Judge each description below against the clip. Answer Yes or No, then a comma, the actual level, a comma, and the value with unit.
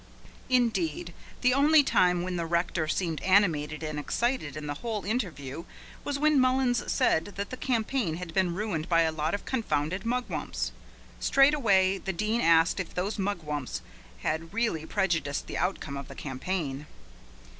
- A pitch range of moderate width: No, wide, 6.3 semitones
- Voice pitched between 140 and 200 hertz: Yes, medium, 185 Hz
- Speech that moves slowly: No, average, 160 wpm